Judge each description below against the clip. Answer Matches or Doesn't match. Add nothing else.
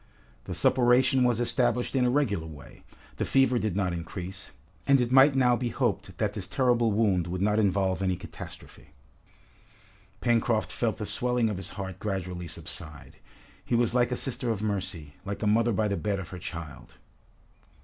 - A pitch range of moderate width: Matches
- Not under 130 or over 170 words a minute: Doesn't match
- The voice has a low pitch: Matches